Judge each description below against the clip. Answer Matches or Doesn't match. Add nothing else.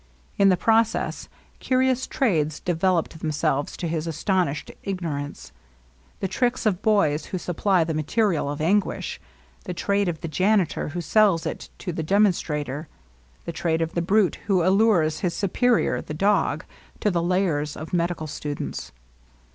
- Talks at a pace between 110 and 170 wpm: Matches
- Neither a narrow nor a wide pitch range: Matches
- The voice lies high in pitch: Doesn't match